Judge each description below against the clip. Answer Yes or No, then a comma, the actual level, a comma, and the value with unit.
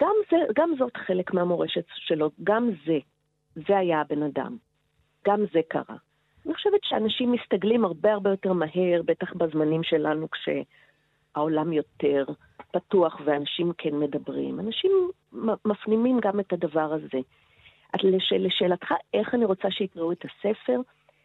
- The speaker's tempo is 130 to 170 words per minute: Yes, average, 135 wpm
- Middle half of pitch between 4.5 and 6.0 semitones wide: Yes, wide, 5.5 semitones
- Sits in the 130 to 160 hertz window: No, medium, 180 Hz